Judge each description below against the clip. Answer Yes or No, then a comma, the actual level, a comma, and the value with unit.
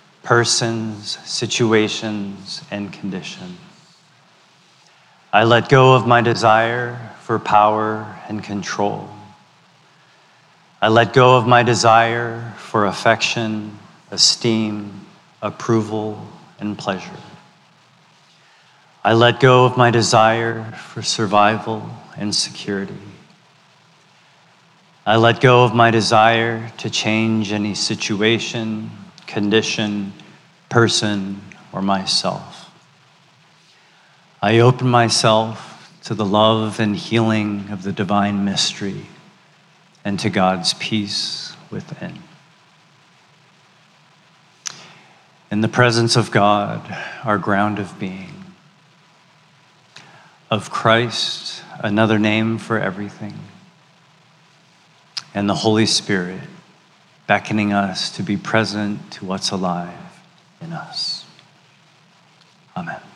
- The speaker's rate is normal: No, slow, 90 wpm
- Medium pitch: No, low, 115 Hz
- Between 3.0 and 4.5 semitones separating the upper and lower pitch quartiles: No, wide, 5.4 semitones